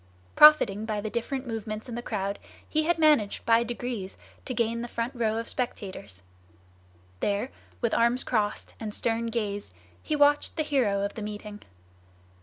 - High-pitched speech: Yes, high, 230 Hz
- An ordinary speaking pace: Yes, average, 165 wpm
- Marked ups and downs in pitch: No, average, 3.1 semitones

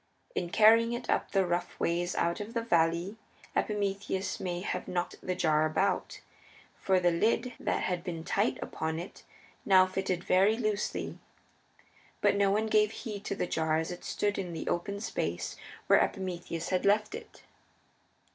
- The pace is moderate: Yes, average, 165 wpm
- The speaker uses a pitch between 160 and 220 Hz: Yes, medium, 185 Hz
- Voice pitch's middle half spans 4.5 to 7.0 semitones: No, average, 3.1 semitones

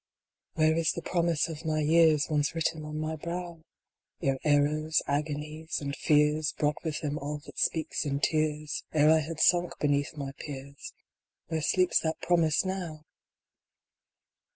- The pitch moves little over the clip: Yes, narrow, 1.6 semitones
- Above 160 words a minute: No, average, 155 wpm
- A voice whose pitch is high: No, medium, 155 Hz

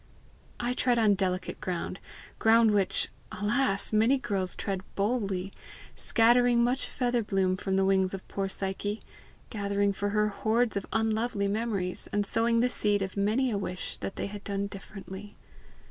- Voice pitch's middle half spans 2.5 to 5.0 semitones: Yes, average, 2.9 semitones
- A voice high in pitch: Yes, high, 205 Hz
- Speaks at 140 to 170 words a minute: Yes, average, 160 wpm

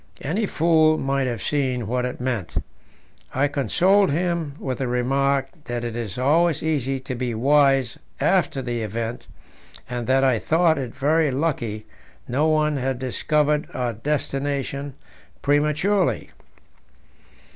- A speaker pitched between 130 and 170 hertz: Yes, low, 135 Hz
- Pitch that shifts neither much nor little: Yes, average, 3.5 semitones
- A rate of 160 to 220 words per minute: No, slow, 135 wpm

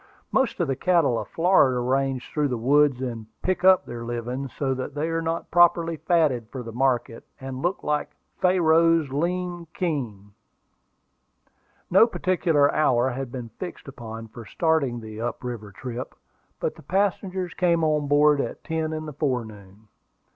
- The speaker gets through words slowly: No, average, 165 wpm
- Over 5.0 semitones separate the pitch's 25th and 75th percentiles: Yes, wide, 5.4 semitones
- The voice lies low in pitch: No, medium, 145 Hz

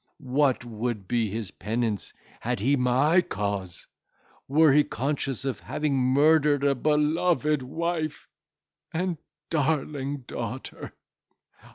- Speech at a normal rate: No, slow, 105 wpm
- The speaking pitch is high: No, low, 135 Hz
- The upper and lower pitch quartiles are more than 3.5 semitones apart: Yes, average, 3.9 semitones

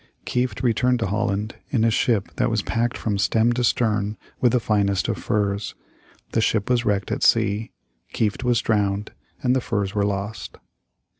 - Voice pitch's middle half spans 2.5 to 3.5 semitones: Yes, average, 2.8 semitones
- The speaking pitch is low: Yes, low, 110 Hz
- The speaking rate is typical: Yes, average, 175 wpm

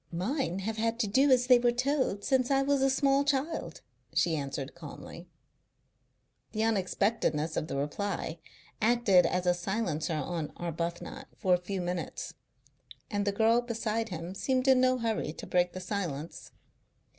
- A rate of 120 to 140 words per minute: No, average, 160 wpm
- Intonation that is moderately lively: No, wide, 6.2 semitones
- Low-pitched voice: No, high, 205 Hz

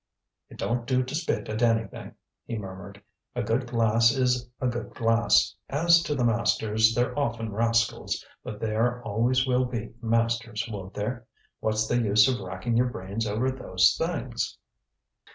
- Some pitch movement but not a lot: No, narrow, 2.2 semitones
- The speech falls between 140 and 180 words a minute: Yes, average, 160 wpm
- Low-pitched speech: Yes, low, 115 Hz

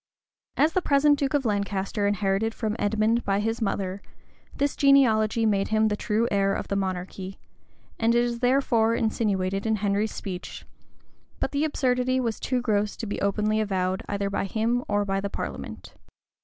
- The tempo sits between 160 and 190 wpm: Yes, average, 170 wpm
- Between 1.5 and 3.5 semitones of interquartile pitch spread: Yes, average, 3.1 semitones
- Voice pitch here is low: No, high, 215 Hz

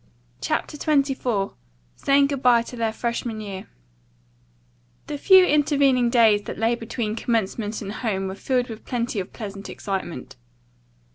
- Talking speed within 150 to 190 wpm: No, average, 140 wpm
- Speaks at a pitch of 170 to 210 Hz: No, high, 235 Hz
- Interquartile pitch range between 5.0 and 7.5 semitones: No, average, 3.8 semitones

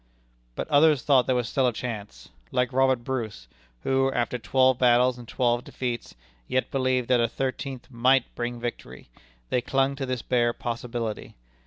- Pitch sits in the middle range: No, low, 125 Hz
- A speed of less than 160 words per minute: No, average, 165 wpm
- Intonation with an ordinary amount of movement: No, narrow, 1.8 semitones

